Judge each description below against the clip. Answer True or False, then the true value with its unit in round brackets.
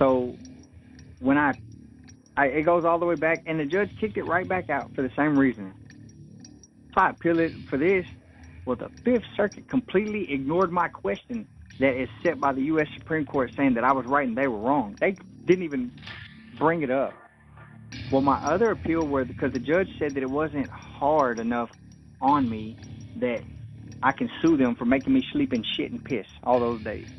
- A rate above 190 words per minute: True (200 wpm)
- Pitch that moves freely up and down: True (6.2 semitones)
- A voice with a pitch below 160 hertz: True (140 Hz)